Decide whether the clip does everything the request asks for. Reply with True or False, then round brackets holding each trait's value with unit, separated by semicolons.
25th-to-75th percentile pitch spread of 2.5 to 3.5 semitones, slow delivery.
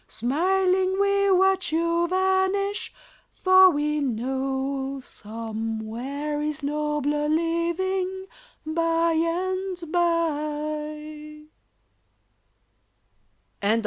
False (4.1 semitones; 65 wpm)